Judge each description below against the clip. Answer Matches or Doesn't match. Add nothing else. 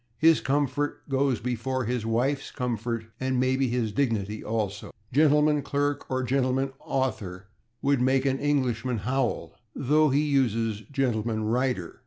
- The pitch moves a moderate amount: Matches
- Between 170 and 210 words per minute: Doesn't match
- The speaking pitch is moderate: Doesn't match